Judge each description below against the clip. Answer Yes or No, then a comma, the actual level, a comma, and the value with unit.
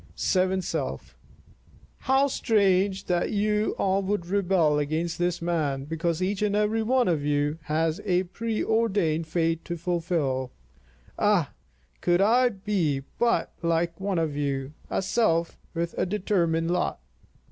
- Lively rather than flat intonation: No, average, 3.9 semitones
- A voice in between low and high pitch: Yes, medium, 175 Hz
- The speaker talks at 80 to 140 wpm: Yes, slow, 135 wpm